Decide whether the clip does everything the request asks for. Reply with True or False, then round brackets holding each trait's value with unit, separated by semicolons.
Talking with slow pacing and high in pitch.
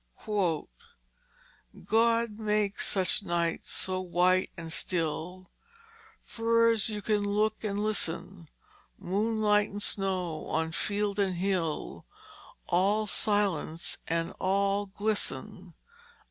True (95 wpm; 200 Hz)